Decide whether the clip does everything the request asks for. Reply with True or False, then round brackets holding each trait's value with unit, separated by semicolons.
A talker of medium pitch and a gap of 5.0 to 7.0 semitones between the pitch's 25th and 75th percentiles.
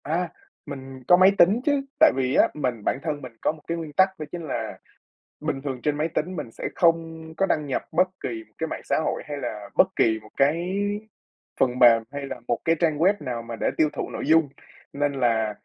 False (145 Hz; 4.6 semitones)